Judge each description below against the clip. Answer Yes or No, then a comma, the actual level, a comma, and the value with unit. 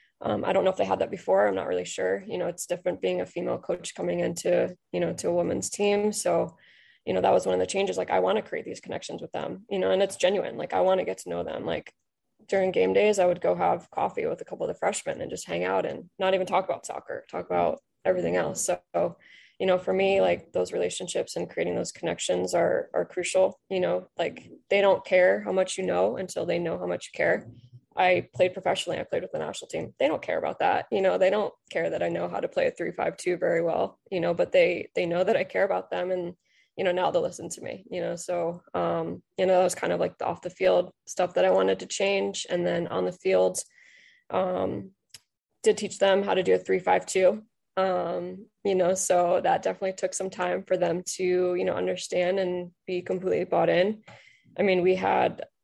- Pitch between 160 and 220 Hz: Yes, medium, 185 Hz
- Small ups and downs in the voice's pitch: Yes, narrow, 2.1 semitones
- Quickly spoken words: Yes, fast, 245 wpm